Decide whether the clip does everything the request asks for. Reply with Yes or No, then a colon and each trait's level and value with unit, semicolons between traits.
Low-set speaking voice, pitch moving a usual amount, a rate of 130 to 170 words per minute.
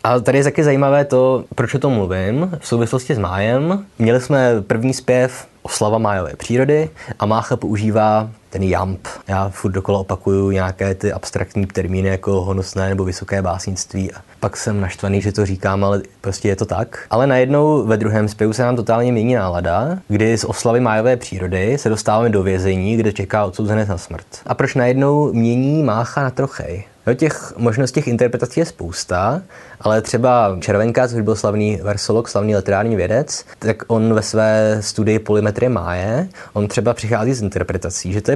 No: low, 110 Hz; average, 4.1 semitones; fast, 180 wpm